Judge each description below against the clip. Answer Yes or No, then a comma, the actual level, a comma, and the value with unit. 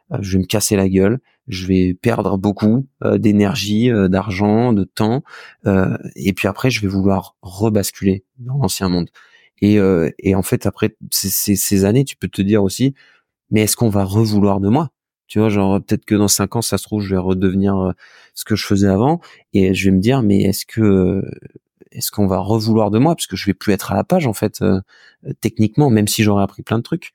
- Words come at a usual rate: Yes, average, 210 wpm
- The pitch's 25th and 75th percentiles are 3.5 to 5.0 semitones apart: No, narrow, 2.4 semitones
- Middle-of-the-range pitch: No, low, 100 Hz